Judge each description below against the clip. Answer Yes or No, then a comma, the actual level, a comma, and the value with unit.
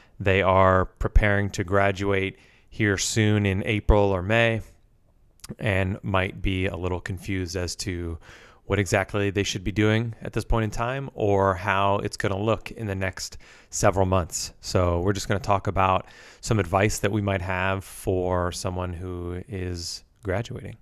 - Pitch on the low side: Yes, low, 100 Hz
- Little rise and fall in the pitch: Yes, narrow, 2.2 semitones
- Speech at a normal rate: Yes, average, 170 wpm